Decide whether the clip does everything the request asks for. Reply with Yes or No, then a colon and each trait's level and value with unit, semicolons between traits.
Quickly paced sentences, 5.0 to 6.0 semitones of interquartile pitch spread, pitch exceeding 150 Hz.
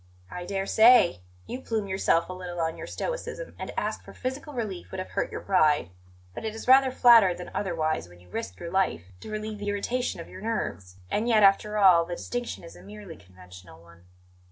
Yes: fast, 215 wpm; average, 5.3 semitones; high, 190 Hz